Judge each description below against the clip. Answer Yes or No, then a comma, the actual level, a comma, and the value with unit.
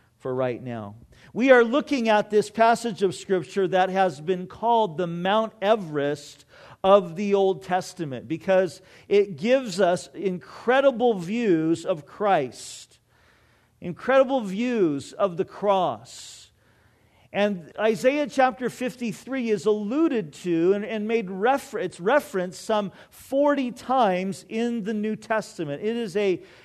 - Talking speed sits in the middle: No, slow, 130 wpm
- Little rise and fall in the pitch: No, average, 4.5 semitones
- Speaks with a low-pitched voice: No, high, 200 Hz